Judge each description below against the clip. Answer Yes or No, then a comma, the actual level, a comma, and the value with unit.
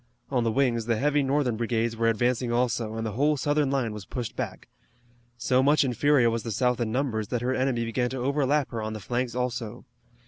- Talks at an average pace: No, fast, 215 wpm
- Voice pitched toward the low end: Yes, low, 125 Hz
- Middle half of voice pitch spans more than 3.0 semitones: No, narrow, 2.6 semitones